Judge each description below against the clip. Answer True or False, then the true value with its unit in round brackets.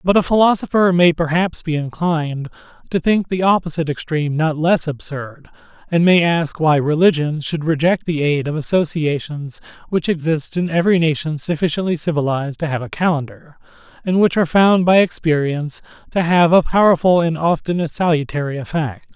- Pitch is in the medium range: True (160 Hz)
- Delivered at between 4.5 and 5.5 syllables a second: True (5.4 syllables/s)